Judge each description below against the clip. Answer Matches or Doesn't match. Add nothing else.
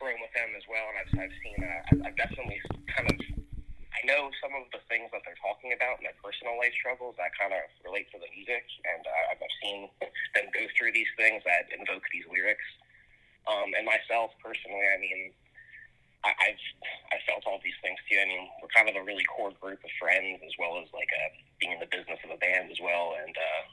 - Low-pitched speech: Matches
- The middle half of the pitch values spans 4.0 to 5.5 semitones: Matches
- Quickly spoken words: Matches